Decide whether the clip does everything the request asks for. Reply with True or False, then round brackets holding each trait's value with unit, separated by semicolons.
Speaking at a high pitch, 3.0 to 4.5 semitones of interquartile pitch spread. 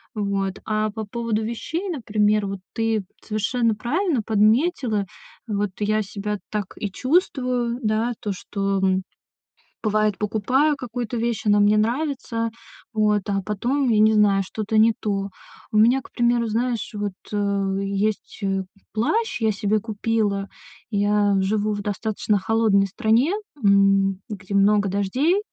False (215 Hz; 2.6 semitones)